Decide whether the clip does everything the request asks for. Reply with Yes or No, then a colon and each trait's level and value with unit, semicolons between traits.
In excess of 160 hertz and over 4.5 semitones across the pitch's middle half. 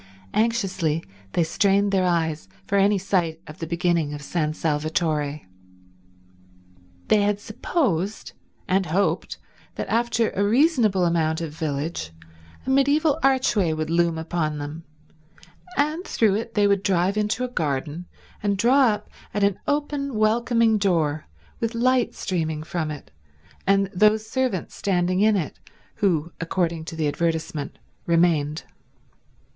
Yes: medium, 185 Hz; average, 5.1 semitones